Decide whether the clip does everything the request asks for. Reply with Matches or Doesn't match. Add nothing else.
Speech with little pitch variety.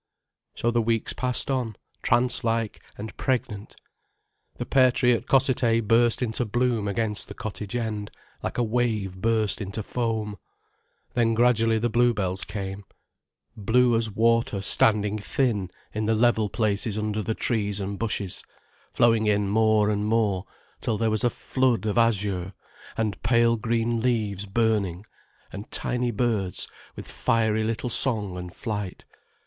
Matches